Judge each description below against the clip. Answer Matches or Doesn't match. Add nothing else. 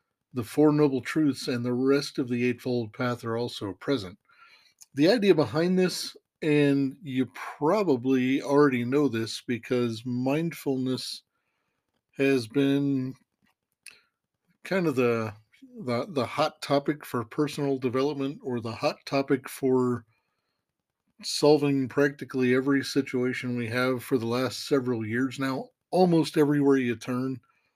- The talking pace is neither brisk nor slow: Doesn't match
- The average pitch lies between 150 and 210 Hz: Doesn't match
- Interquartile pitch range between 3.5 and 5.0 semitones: Doesn't match